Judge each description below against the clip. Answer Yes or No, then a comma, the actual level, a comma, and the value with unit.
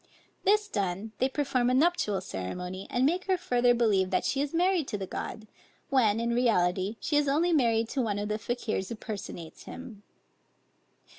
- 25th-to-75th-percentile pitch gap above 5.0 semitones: Yes, wide, 5.4 semitones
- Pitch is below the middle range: No, high, 235 Hz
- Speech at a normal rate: Yes, average, 180 wpm